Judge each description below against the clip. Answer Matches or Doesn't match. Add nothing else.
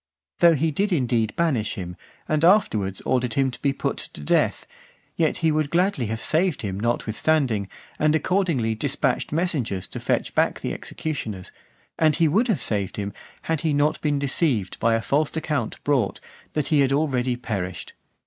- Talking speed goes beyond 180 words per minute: Doesn't match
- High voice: Doesn't match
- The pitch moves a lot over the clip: Matches